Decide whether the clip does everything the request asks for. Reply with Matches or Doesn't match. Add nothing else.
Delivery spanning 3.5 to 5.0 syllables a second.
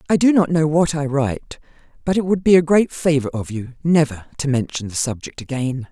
Doesn't match